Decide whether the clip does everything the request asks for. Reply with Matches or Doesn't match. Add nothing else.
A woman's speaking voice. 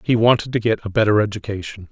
Doesn't match